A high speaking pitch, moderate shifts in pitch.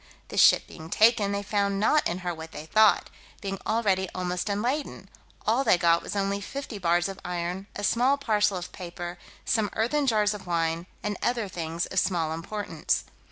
Yes: high, 195 Hz; average, 3.6 semitones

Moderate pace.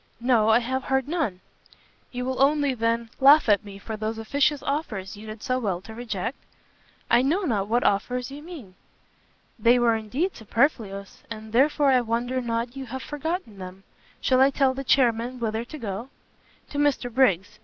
Yes: average, 180 wpm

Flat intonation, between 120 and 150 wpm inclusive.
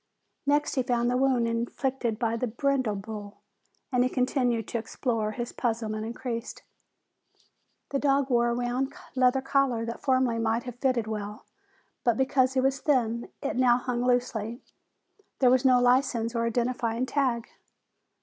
No: narrow, 2.0 semitones; average, 160 wpm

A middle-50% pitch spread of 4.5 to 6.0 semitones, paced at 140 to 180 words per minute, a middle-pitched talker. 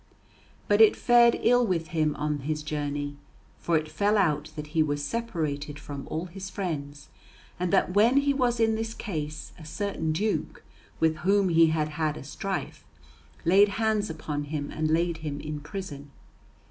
Yes: average, 5.2 semitones; average, 170 wpm; medium, 160 Hz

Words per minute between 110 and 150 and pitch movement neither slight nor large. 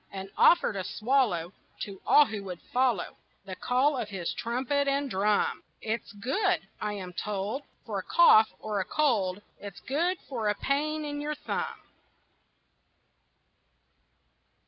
No: average, 145 wpm; wide, 6.1 semitones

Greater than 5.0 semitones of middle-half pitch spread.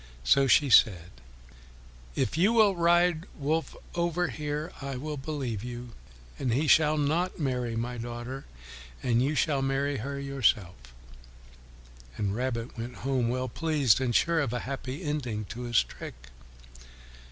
No: average, 4.2 semitones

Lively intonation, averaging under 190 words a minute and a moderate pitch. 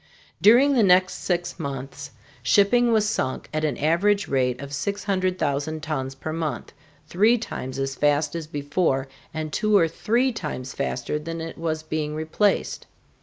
Yes: wide, 5.7 semitones; average, 155 wpm; medium, 160 Hz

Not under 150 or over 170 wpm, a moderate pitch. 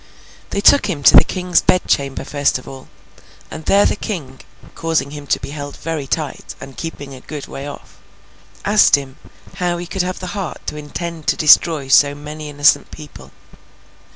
No: average, 185 wpm; medium, 150 Hz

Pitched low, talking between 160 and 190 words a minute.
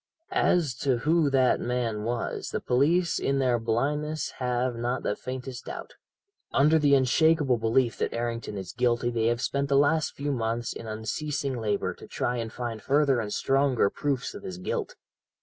Yes: low, 125 Hz; average, 175 wpm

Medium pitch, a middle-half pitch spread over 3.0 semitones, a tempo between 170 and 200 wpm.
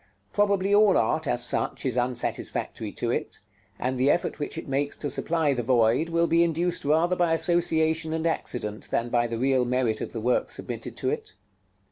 Yes: medium, 145 Hz; wide, 5.4 semitones; average, 190 wpm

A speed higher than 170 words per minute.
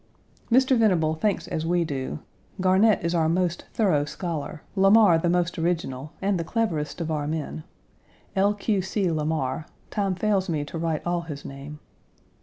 No: average, 165 wpm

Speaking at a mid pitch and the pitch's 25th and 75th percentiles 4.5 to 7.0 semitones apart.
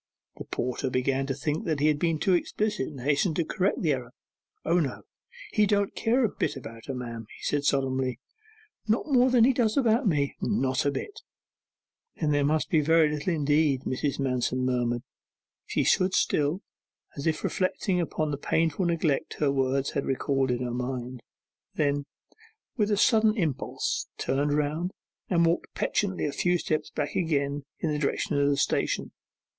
Yes: medium, 150 Hz; average, 4.8 semitones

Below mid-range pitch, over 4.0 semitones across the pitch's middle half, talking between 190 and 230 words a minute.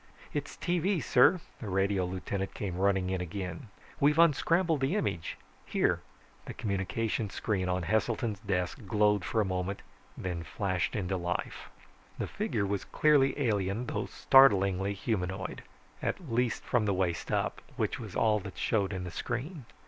No: low, 100 Hz; average, 4.8 semitones; average, 155 wpm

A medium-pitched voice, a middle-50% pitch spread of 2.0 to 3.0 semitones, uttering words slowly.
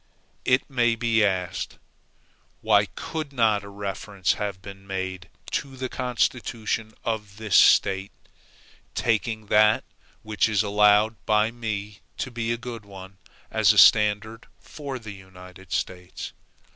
No: low, 105 Hz; average, 2.7 semitones; slow, 130 wpm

